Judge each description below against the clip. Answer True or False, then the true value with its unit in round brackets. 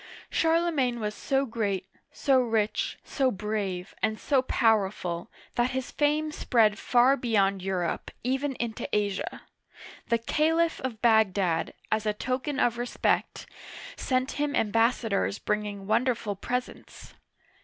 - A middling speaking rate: False (125 wpm)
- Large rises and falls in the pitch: False (3.9 semitones)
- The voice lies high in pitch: True (230 Hz)